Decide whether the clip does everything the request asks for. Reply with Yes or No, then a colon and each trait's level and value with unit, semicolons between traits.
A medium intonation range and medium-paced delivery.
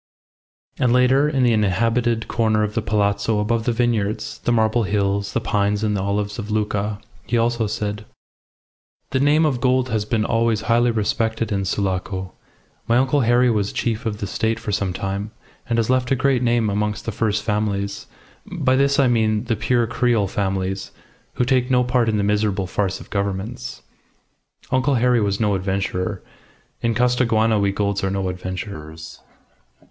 Yes: average, 3.0 semitones; average, 175 wpm